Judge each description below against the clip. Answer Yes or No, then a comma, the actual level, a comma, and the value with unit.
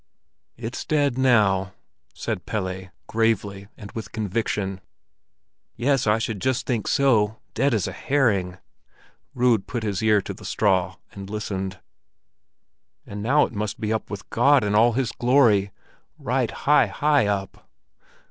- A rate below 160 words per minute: Yes, average, 140 wpm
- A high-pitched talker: No, low, 110 Hz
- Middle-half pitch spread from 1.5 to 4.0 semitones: Yes, average, 3.5 semitones